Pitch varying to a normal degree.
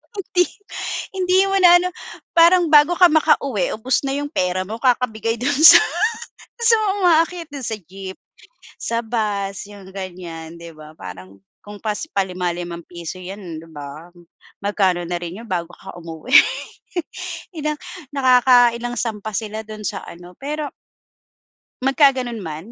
No: wide, 7.8 semitones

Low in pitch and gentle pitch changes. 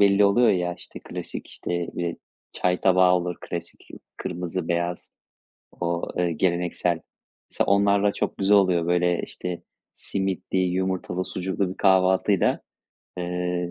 Yes: very low, 90 Hz; narrow, 1.5 semitones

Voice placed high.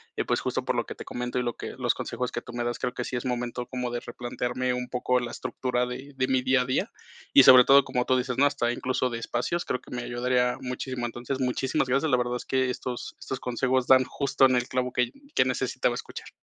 No: low, 125 Hz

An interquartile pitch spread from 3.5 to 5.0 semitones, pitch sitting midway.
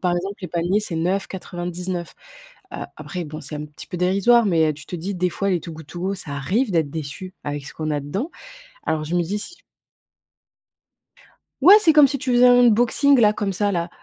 Yes: average, 4.3 semitones; medium, 180 Hz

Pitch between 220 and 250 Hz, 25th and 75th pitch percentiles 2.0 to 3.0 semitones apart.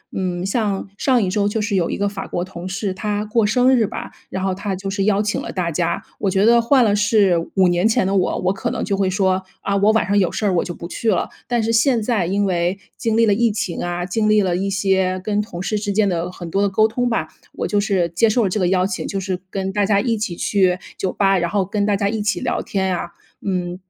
No: high, 200 Hz; narrow, 2.4 semitones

